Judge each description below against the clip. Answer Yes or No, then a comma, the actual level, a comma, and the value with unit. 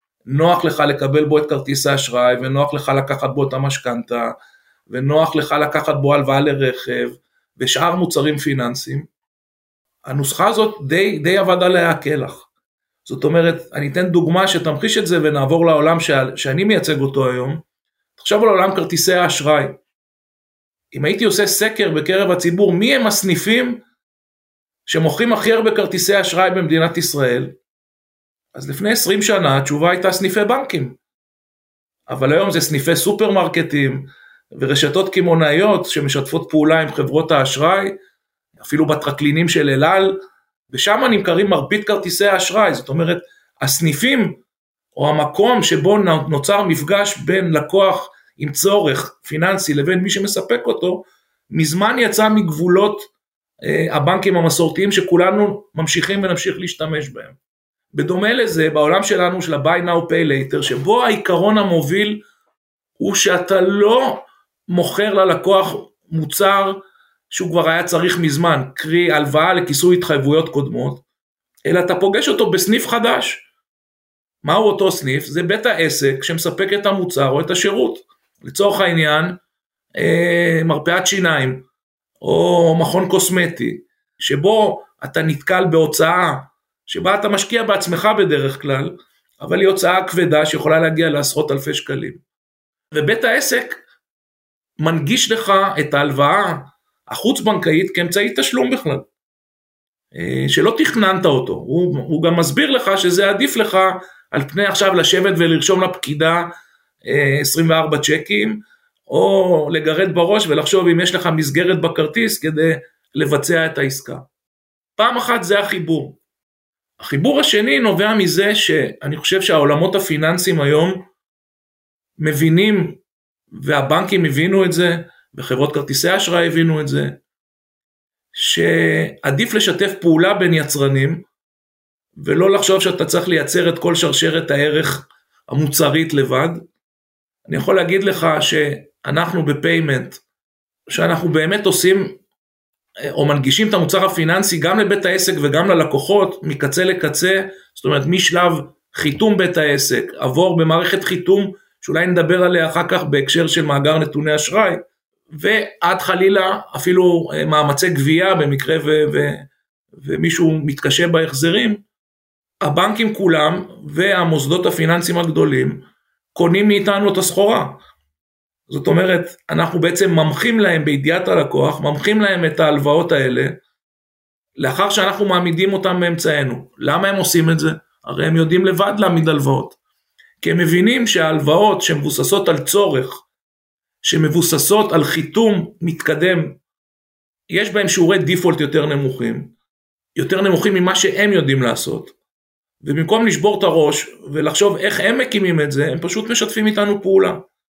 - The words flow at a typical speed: Yes, average, 120 wpm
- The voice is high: No, medium, 170 Hz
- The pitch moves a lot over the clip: No, average, 4.3 semitones